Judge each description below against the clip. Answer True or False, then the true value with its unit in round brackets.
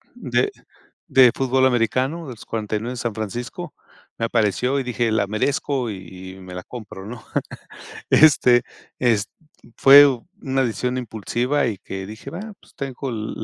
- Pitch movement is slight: False (3.5 semitones)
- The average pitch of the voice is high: False (120 Hz)